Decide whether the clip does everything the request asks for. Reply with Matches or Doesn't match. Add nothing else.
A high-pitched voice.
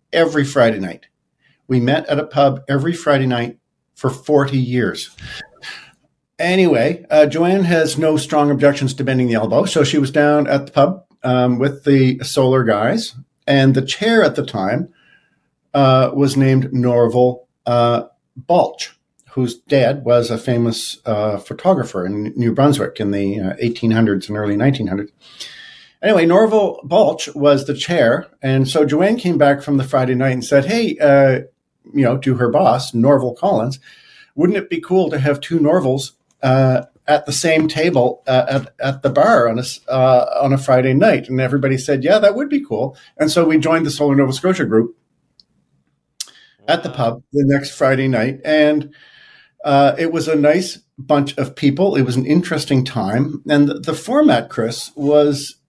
Doesn't match